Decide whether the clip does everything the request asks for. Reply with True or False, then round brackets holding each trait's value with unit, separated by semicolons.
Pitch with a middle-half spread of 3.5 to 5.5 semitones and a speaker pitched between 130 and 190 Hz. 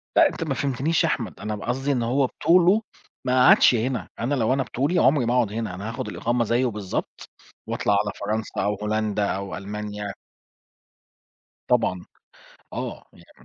False (4.2 semitones; 115 Hz)